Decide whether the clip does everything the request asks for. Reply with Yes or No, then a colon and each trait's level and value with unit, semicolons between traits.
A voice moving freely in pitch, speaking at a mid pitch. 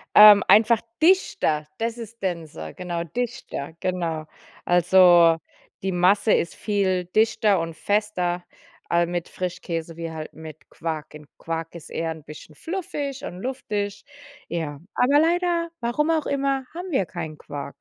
Yes: wide, 6.0 semitones; medium, 180 Hz